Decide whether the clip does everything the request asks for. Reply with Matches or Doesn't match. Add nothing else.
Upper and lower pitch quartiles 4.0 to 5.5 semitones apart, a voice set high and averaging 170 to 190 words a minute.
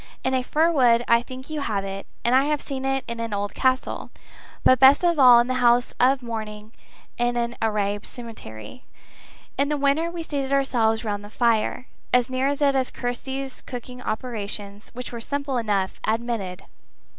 Doesn't match